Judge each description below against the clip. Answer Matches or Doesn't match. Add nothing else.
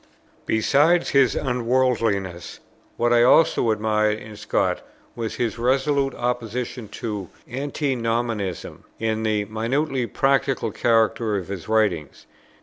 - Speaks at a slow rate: Matches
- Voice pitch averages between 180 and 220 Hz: Doesn't match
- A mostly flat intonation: Doesn't match